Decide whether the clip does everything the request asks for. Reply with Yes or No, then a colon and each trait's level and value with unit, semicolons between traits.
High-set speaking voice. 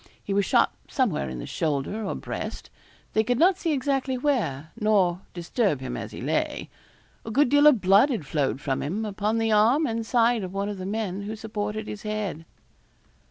Yes: high, 210 Hz